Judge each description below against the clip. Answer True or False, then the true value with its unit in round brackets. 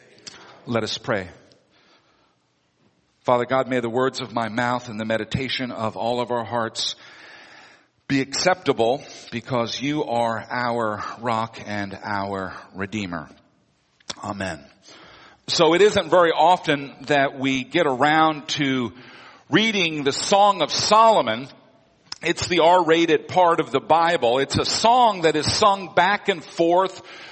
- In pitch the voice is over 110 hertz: True (135 Hz)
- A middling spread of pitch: False (6.2 semitones)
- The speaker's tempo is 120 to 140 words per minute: True (135 wpm)